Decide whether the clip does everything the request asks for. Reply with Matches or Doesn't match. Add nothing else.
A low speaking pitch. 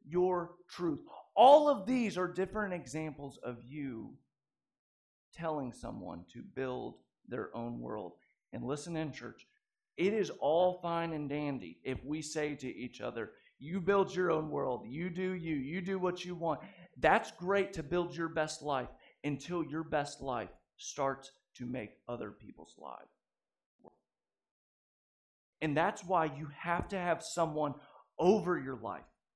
Doesn't match